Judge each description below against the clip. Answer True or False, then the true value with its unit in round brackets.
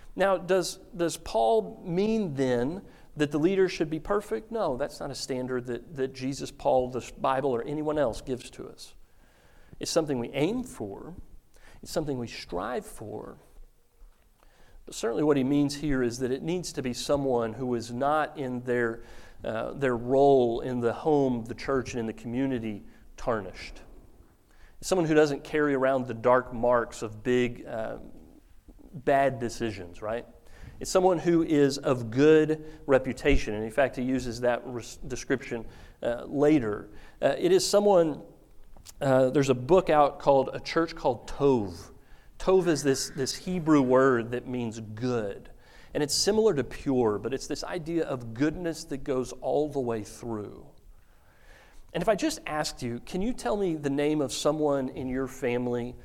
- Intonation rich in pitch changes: False (4.3 semitones)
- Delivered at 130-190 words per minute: True (170 wpm)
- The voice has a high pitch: False (135 Hz)